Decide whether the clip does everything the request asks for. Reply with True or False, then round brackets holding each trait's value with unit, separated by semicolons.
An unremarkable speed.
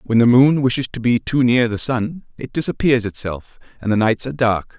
False (225 wpm)